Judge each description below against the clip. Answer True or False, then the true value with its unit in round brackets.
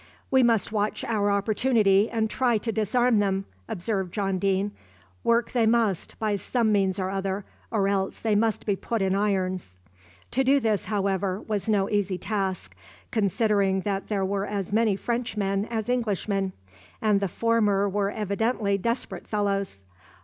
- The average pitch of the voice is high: True (205 Hz)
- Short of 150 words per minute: False (155 wpm)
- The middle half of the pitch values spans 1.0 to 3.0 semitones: True (2.4 semitones)